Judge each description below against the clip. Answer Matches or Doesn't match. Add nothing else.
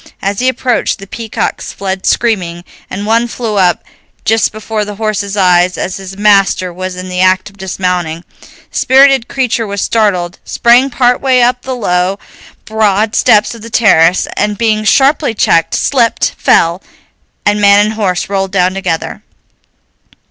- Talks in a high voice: Matches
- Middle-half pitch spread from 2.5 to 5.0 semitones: Matches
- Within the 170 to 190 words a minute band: Doesn't match